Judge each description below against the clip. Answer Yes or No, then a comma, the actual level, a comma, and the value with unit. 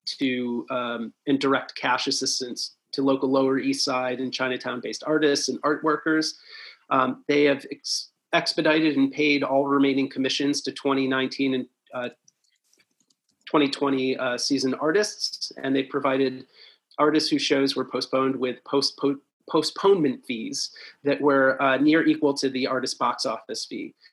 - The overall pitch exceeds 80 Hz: Yes, low, 135 Hz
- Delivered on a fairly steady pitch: Yes, narrow, 1.8 semitones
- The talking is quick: No, average, 145 wpm